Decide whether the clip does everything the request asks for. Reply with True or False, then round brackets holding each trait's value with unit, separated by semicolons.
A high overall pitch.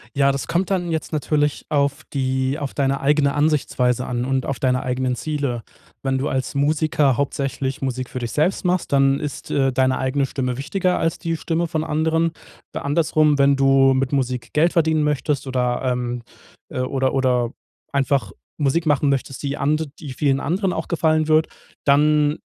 False (140 Hz)